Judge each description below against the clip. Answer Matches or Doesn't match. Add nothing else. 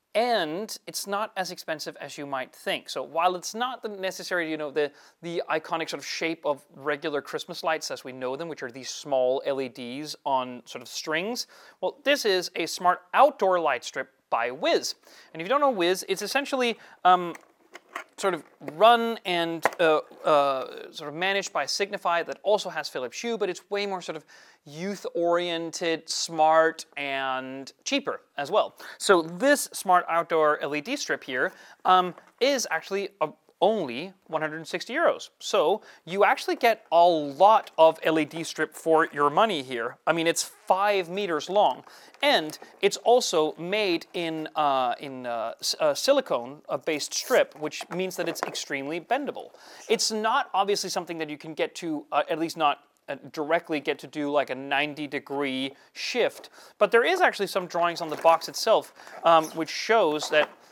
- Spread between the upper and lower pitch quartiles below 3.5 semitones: Doesn't match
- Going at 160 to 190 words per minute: Matches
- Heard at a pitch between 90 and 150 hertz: Doesn't match